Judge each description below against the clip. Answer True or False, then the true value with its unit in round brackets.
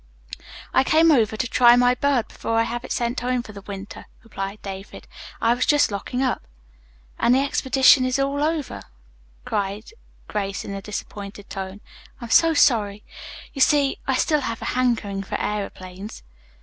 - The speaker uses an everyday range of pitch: True (4.6 semitones)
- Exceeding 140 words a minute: True (170 wpm)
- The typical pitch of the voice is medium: False (235 Hz)